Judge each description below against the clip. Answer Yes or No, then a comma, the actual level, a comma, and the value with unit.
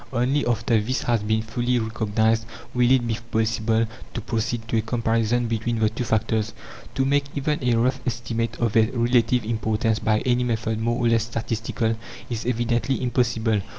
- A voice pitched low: Yes, low, 115 Hz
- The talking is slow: No, average, 175 wpm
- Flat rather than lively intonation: Yes, narrow, 1.5 semitones